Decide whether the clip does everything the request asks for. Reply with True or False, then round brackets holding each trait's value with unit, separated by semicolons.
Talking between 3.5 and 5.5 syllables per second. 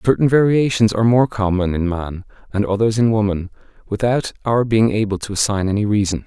False (5.7 syllables/s)